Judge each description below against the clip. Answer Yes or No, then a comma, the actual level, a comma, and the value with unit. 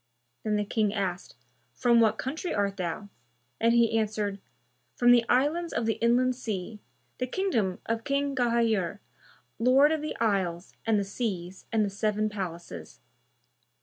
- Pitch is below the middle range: No, high, 220 Hz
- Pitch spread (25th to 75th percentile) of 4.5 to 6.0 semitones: No, average, 3.6 semitones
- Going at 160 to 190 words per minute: No, average, 150 wpm